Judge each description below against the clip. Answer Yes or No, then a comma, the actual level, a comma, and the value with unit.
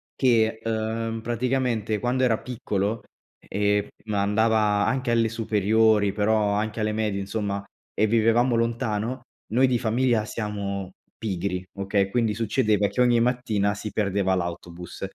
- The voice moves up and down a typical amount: No, narrow, 2.2 semitones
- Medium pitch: No, low, 110 Hz